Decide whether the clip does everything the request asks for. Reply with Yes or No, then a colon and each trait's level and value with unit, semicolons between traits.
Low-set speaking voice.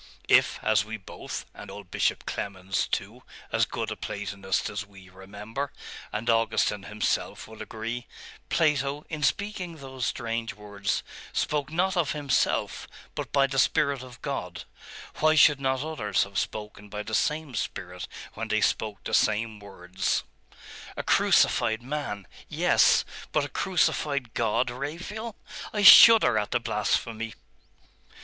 Yes: low, 115 Hz